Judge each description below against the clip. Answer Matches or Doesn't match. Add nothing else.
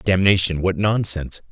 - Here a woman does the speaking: Doesn't match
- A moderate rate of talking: Doesn't match